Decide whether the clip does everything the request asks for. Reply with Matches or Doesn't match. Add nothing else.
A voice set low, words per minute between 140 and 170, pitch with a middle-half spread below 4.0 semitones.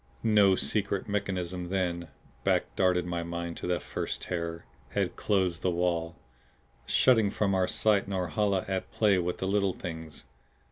Matches